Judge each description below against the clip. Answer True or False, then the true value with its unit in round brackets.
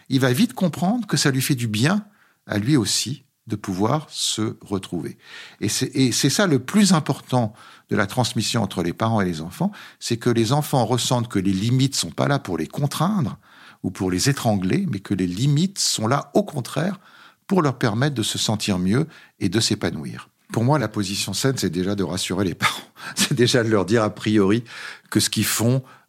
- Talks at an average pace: True (210 wpm)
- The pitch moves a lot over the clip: True (6.0 semitones)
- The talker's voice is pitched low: True (120 Hz)